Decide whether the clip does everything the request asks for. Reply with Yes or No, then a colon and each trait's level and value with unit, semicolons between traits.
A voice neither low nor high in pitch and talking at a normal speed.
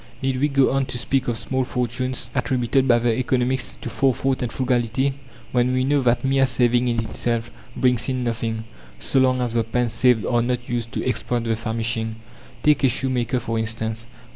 No: low, 125 Hz; average, 190 wpm